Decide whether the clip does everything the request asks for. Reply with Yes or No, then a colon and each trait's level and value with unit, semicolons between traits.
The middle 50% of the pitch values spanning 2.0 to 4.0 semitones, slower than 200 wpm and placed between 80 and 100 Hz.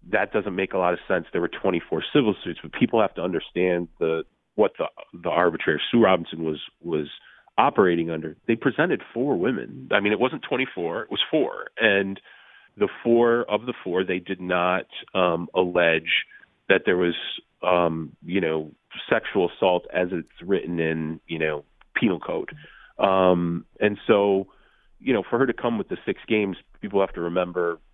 Yes: average, 2.9 semitones; average, 185 wpm; very low, 90 Hz